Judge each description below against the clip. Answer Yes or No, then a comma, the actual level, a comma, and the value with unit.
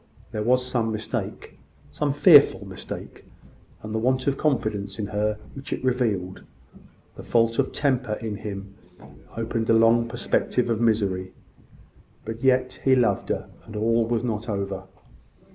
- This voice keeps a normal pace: Yes, average, 150 wpm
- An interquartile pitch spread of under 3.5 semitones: Yes, average, 3.1 semitones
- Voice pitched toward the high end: No, low, 115 Hz